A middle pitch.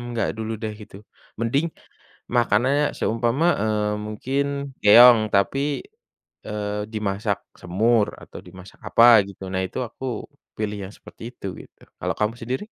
No: low, 110 Hz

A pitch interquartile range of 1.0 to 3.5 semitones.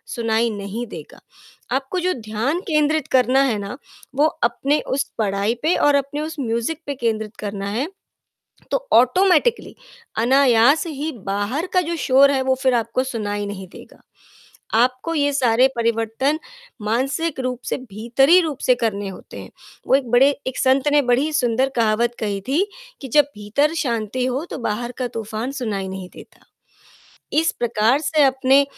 No: average, 4.2 semitones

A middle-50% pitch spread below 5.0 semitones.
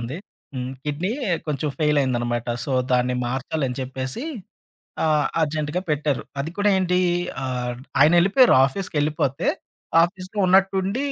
No: wide, 5.6 semitones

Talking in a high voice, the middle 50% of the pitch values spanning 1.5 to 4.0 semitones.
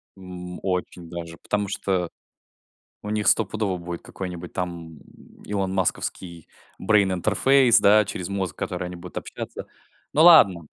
No: very low, 95 Hz; average, 2.7 semitones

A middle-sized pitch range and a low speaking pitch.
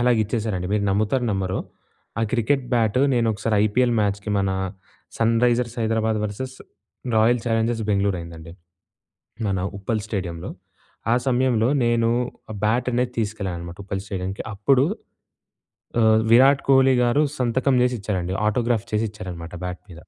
Yes: average, 3.5 semitones; low, 110 Hz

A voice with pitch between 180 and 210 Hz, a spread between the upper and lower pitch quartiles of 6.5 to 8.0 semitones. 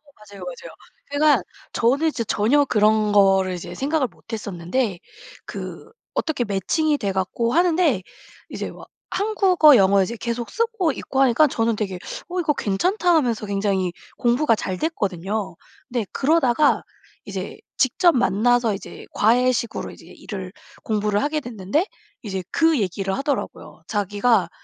No: high, 230 Hz; wide, 6.8 semitones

